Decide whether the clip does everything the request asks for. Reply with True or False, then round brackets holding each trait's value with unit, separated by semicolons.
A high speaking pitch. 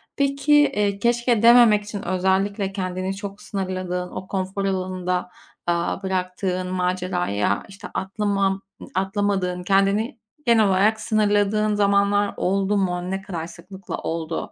True (195 Hz)